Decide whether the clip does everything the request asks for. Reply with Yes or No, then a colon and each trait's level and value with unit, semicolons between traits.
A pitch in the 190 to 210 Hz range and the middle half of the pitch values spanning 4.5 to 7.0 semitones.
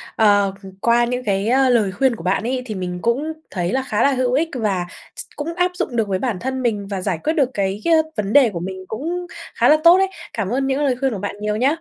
No: high, 235 Hz; average, 5.2 semitones